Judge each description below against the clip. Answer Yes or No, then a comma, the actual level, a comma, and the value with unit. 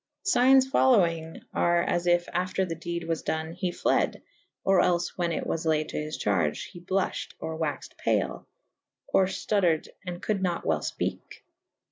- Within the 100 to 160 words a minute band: No, average, 180 wpm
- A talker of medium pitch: Yes, medium, 175 Hz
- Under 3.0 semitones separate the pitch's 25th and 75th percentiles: Yes, narrow, 2.6 semitones